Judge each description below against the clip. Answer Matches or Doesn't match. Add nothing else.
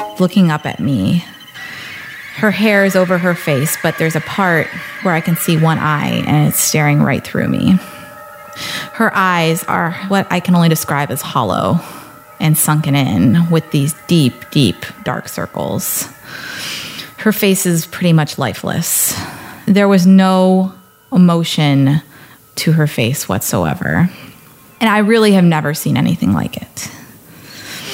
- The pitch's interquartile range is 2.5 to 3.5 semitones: Doesn't match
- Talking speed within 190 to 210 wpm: Doesn't match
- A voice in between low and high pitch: Matches